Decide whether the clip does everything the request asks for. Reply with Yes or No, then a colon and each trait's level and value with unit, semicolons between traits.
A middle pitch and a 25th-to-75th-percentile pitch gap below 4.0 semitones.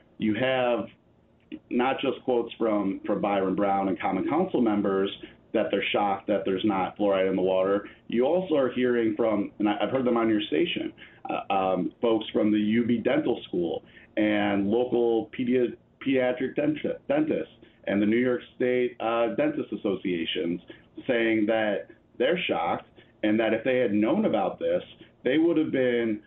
No: low, 110 Hz; average, 3.3 semitones